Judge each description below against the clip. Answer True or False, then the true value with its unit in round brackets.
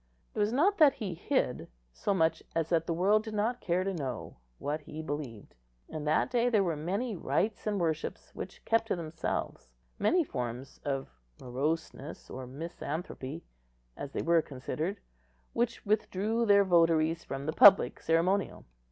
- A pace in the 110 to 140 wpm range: False (160 wpm)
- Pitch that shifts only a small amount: False (5.6 semitones)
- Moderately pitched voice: True (170 Hz)